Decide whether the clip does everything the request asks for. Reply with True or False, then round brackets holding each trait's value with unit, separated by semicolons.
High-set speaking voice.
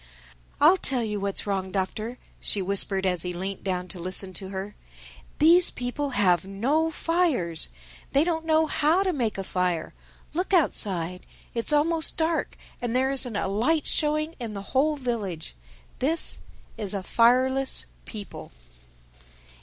True (235 Hz)